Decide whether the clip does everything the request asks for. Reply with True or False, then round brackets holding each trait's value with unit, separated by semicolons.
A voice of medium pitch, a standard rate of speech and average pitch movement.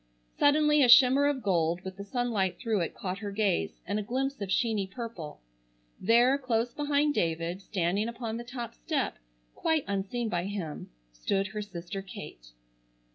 False (215 Hz; 165 wpm; 4.8 semitones)